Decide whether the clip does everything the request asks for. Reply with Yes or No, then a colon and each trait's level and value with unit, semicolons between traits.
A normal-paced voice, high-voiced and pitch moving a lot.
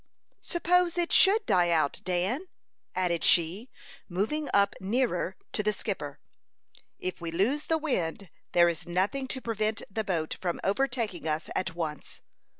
Yes: average, 150 wpm; high, 195 Hz; wide, 7.1 semitones